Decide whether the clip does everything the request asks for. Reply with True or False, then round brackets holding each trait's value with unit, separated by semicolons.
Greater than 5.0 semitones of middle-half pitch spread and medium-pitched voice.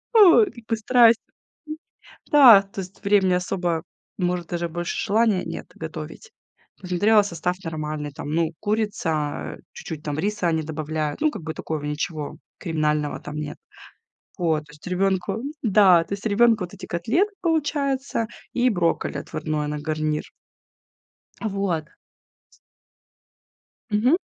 True (5.6 semitones; 180 Hz)